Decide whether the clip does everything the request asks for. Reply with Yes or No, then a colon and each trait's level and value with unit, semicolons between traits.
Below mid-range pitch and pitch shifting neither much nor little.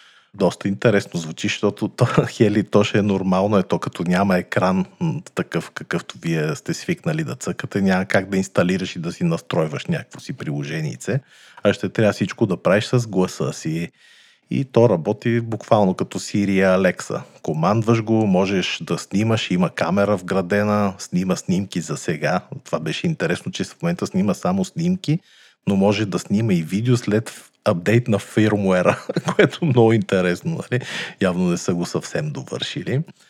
No: low, 105 Hz; wide, 7.8 semitones